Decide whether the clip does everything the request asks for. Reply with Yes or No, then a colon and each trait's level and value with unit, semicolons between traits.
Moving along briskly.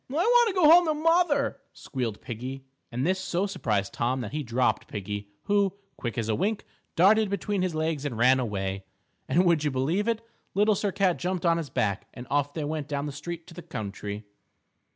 Yes: fast, 210 wpm